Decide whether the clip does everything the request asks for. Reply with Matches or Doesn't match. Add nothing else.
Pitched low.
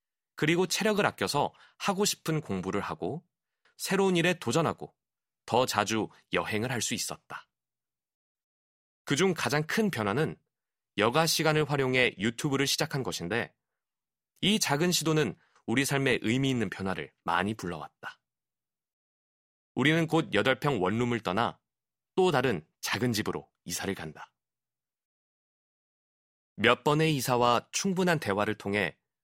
Matches